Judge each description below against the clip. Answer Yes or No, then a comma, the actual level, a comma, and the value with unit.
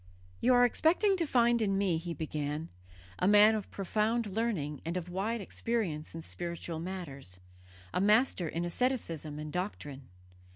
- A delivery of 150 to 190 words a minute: Yes, average, 155 wpm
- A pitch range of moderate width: No, wide, 6.0 semitones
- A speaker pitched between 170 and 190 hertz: Yes, medium, 185 Hz